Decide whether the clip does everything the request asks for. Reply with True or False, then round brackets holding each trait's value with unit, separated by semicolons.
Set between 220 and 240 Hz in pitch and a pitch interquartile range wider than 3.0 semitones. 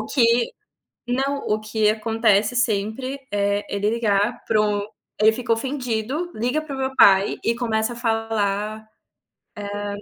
False (225 Hz; 2.7 semitones)